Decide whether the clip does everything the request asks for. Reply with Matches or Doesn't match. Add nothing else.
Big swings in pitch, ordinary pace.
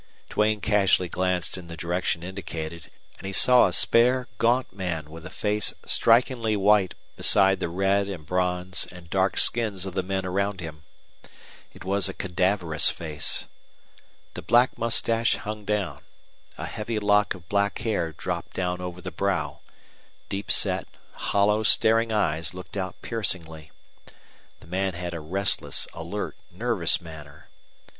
Doesn't match